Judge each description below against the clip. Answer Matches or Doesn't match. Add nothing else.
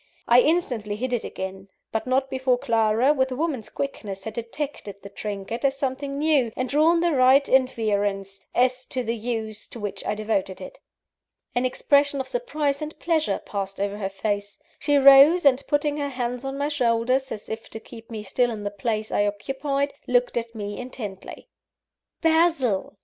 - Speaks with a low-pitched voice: Doesn't match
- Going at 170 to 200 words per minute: Matches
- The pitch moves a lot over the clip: Doesn't match